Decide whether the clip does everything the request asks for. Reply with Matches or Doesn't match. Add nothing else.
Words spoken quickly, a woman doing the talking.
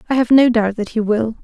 Matches